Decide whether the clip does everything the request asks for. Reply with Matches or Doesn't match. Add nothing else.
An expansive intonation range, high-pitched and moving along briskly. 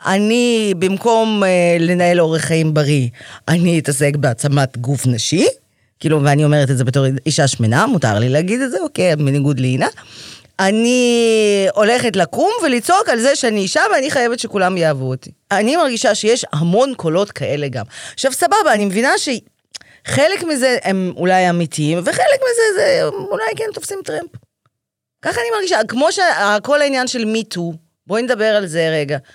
Matches